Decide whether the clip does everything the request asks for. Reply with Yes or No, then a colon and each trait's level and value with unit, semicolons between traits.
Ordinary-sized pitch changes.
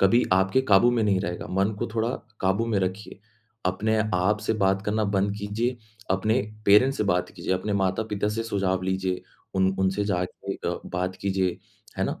No: narrow, 2.3 semitones